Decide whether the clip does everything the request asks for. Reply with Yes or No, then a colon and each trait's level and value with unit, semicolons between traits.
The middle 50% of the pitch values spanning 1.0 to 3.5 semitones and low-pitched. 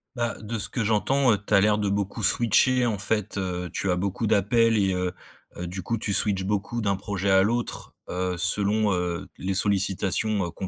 Yes: narrow, 2.6 semitones; low, 100 Hz